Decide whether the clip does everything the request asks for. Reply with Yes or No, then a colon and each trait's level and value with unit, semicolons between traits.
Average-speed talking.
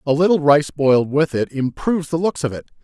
No: fast, 235 wpm